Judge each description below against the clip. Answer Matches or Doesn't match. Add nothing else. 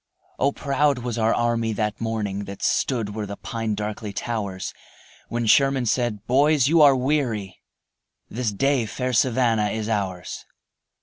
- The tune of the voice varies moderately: Matches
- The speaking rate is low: Doesn't match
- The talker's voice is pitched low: Matches